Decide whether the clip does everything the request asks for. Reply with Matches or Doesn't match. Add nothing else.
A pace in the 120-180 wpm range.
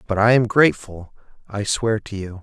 Doesn't match